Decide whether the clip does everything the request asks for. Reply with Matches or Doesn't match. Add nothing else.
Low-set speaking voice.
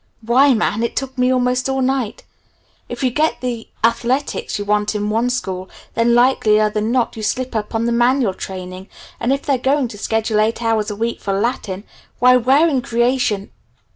Doesn't match